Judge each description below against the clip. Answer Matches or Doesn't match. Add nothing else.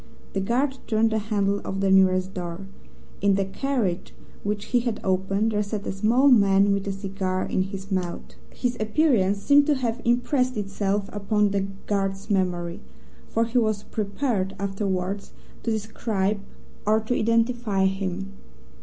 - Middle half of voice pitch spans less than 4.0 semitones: Matches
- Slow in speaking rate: Doesn't match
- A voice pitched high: Matches